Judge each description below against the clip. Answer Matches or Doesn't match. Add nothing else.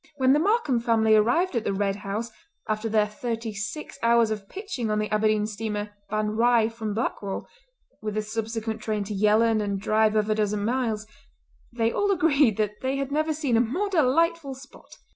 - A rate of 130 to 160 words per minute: Doesn't match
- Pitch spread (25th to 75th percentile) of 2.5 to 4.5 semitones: Matches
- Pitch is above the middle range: Matches